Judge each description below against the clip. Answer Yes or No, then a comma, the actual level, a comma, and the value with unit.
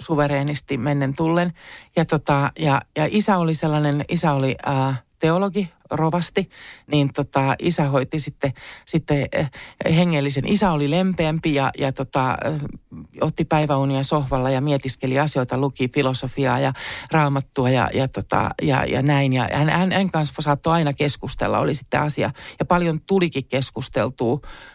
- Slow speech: No, average, 145 wpm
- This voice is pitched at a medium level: Yes, medium, 145 Hz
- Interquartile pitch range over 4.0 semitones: No, average, 3.1 semitones